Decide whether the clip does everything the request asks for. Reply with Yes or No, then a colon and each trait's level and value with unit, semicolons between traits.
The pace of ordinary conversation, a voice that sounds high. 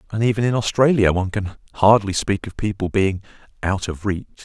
No: average, 190 wpm; low, 100 Hz